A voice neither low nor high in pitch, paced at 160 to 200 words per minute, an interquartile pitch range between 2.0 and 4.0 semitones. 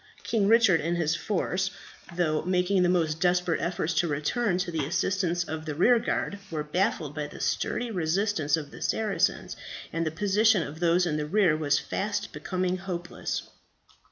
Yes: medium, 175 Hz; average, 170 wpm; average, 3.6 semitones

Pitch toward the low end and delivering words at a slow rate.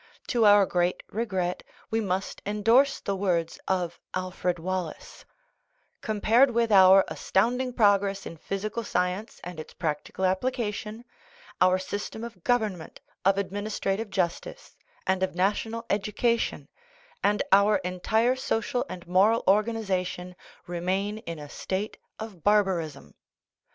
No: high, 195 Hz; slow, 125 wpm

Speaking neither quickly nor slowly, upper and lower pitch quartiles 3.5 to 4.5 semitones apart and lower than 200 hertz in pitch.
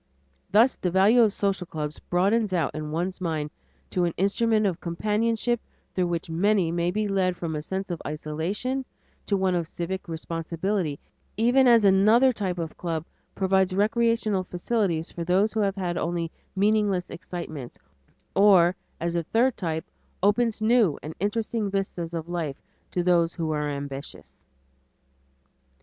Yes: average, 155 wpm; average, 4.0 semitones; medium, 185 Hz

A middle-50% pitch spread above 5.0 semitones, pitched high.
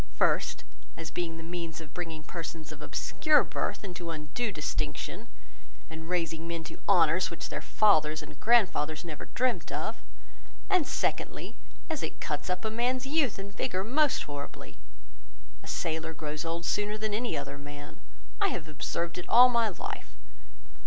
No: wide, 5.4 semitones; medium, 170 Hz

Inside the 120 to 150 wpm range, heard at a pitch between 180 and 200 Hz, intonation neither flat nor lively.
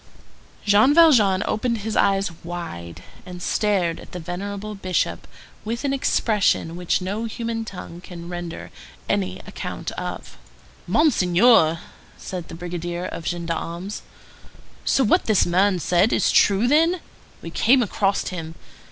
Yes: slow, 135 wpm; high, 190 Hz; average, 4.0 semitones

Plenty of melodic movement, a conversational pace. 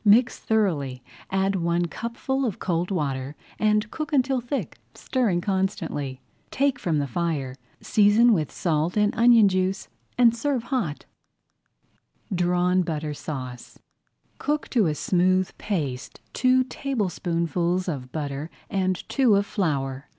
No: wide, 6.6 semitones; slow, 130 wpm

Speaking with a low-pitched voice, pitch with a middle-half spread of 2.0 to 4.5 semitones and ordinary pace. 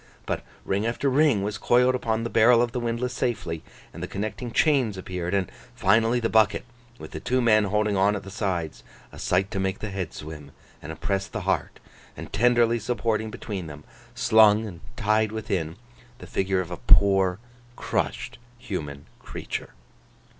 Yes: low, 105 Hz; average, 3.7 semitones; average, 170 wpm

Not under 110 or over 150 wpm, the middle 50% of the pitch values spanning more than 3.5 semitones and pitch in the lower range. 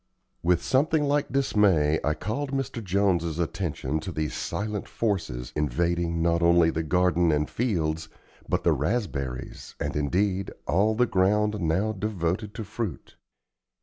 Yes: average, 140 wpm; average, 4.7 semitones; very low, 90 Hz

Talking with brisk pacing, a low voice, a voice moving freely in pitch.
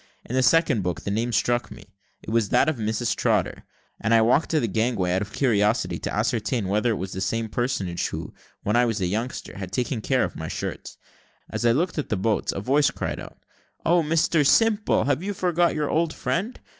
Yes: fast, 225 wpm; low, 120 Hz; wide, 6.1 semitones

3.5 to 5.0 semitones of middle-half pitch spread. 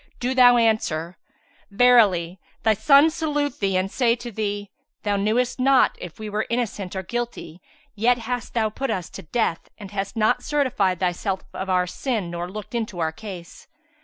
Yes: average, 4.6 semitones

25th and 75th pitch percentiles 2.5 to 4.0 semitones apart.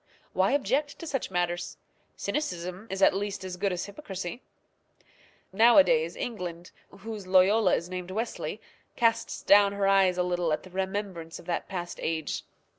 Yes: average, 3.6 semitones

